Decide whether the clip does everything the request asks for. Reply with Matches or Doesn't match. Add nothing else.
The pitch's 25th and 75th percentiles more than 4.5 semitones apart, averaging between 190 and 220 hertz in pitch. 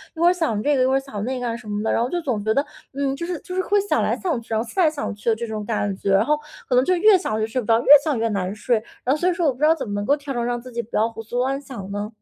Doesn't match